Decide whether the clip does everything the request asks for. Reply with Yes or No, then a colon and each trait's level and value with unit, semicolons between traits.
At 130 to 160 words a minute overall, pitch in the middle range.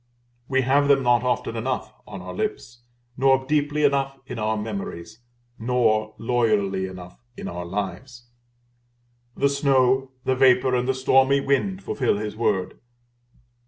No: average, 140 wpm; low, 125 Hz